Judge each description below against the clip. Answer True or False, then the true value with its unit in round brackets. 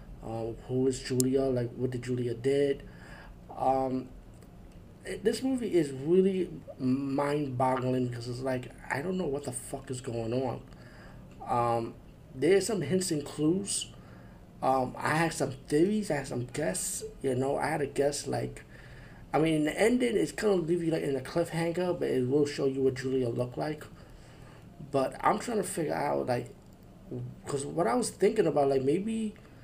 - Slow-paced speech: False (175 wpm)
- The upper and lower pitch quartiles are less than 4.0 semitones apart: False (4.6 semitones)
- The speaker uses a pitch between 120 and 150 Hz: True (135 Hz)